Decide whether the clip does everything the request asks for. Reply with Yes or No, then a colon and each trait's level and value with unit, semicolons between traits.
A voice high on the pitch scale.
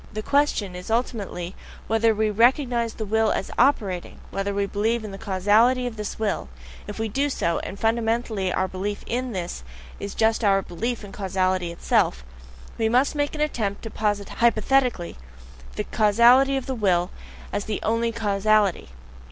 Yes: high, 215 Hz